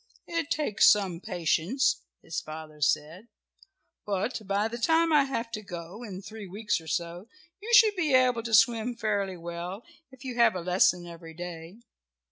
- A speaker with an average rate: Yes, average, 170 wpm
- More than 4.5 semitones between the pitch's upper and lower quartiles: Yes, wide, 5.6 semitones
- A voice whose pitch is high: Yes, high, 205 Hz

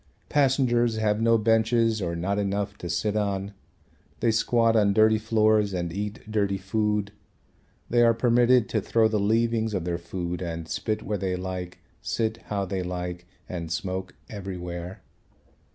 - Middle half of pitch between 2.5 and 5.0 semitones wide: Yes, average, 3.4 semitones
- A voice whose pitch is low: Yes, low, 105 Hz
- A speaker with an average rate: Yes, average, 155 wpm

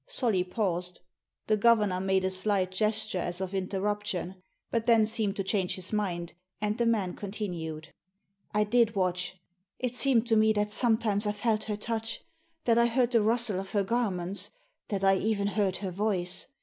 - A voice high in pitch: Yes, high, 205 Hz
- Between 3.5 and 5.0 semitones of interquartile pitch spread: No, average, 3.0 semitones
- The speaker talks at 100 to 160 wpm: No, average, 180 wpm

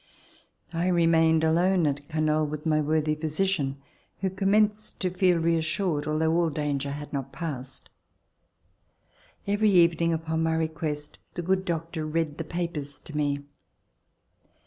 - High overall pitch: No, medium, 160 Hz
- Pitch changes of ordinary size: No, narrow, 2.3 semitones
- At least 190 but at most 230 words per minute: No, slow, 135 wpm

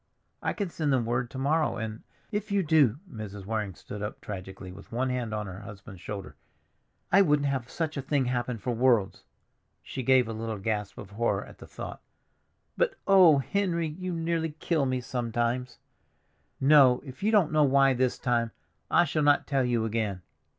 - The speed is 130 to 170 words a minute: No, average, 185 wpm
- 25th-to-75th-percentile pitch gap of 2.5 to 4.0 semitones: No, average, 5.3 semitones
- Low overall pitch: Yes, low, 125 Hz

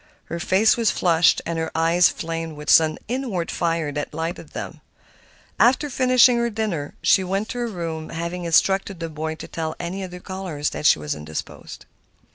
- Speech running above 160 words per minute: Yes, average, 180 wpm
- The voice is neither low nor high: Yes, medium, 170 Hz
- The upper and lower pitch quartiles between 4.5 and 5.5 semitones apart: No, average, 3.4 semitones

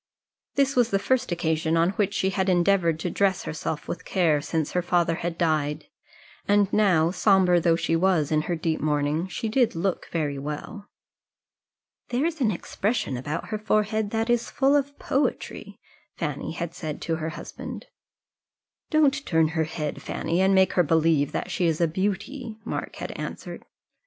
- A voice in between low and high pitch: Yes, medium, 175 Hz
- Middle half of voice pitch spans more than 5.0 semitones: No, average, 4.7 semitones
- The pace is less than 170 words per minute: No, average, 175 wpm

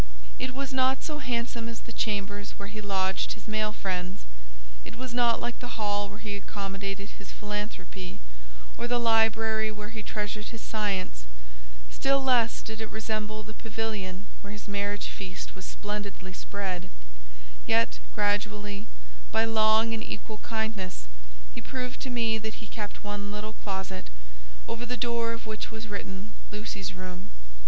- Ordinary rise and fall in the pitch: No, narrow, 2.0 semitones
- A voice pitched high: Yes, high, 215 Hz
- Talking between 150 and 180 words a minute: Yes, average, 160 wpm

